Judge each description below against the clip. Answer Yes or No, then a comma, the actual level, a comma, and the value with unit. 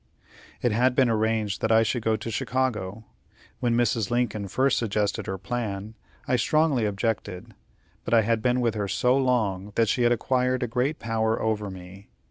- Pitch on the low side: Yes, low, 115 Hz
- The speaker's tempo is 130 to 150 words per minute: No, average, 175 wpm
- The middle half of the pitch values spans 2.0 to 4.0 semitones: Yes, average, 2.9 semitones